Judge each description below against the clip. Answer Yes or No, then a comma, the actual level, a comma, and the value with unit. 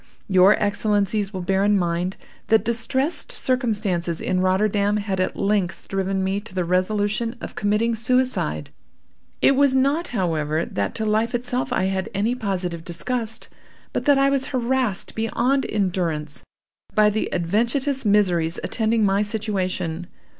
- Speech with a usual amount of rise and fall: Yes, average, 4.1 semitones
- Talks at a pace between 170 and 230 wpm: No, average, 145 wpm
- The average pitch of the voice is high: Yes, high, 205 Hz